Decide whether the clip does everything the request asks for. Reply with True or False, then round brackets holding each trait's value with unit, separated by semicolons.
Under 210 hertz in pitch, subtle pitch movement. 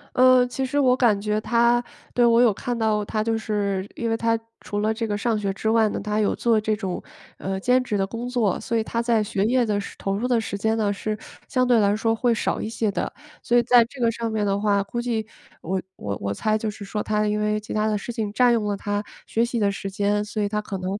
False (215 Hz; 2.3 semitones)